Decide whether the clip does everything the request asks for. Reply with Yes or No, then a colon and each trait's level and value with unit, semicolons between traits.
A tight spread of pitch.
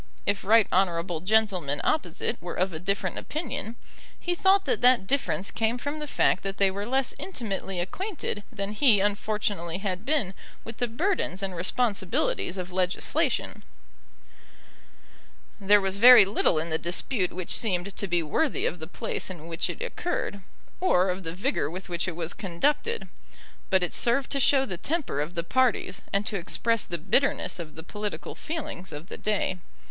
No: wide, 5.4 semitones